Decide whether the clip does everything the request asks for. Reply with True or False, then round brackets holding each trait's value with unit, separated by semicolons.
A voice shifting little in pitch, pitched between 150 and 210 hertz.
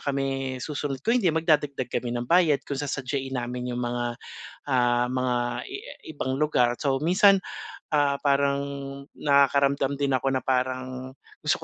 False (2.2 semitones; 135 Hz)